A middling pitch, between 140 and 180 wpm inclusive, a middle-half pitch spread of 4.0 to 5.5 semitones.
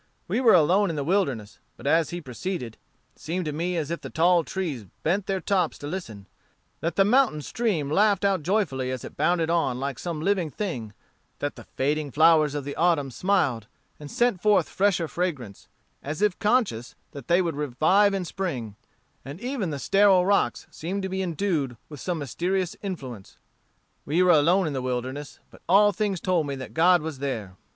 No: medium, 165 Hz; average, 190 wpm; average, 5.2 semitones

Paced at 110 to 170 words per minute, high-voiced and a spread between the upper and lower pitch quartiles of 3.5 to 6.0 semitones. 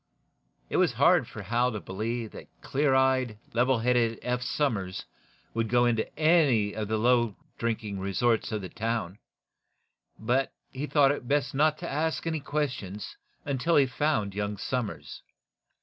No: average, 155 wpm; low, 120 Hz; average, 4.1 semitones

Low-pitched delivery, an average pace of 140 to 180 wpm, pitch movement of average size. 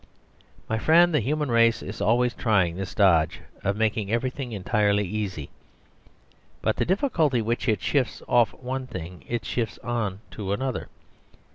Yes: low, 115 Hz; average, 150 wpm; average, 4.1 semitones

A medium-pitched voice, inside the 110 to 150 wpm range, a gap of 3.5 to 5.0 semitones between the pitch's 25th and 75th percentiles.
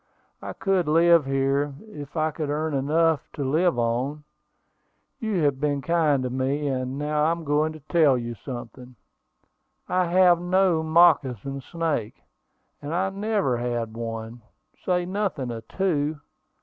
Yes: medium, 150 Hz; average, 145 wpm; average, 4.4 semitones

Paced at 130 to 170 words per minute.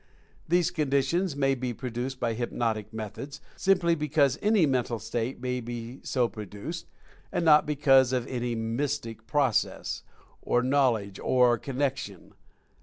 Yes: average, 140 wpm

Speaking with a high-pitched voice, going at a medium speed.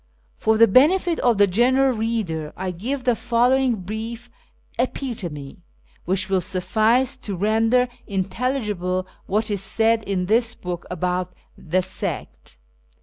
No: high, 220 Hz; slow, 130 wpm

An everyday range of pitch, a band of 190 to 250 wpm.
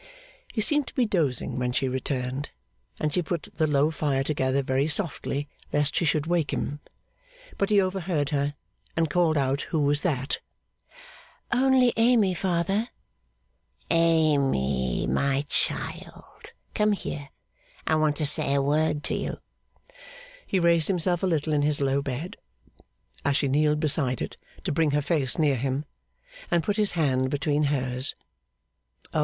No: average, 3.6 semitones; average, 155 wpm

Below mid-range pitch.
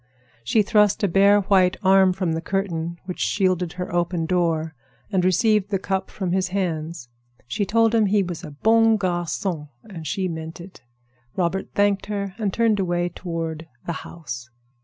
No: medium, 185 Hz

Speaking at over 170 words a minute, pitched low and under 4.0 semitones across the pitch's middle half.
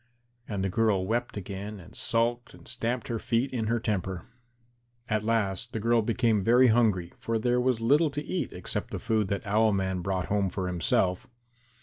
Yes: average, 190 wpm; low, 110 Hz; average, 3.5 semitones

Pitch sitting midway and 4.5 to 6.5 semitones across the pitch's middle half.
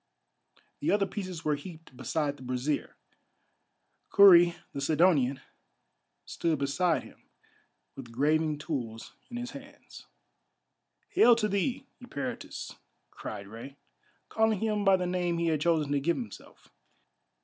Yes: medium, 165 Hz; wide, 5.6 semitones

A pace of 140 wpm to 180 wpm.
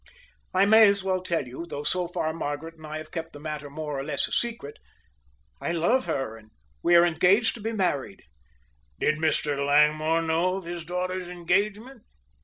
No: average, 190 wpm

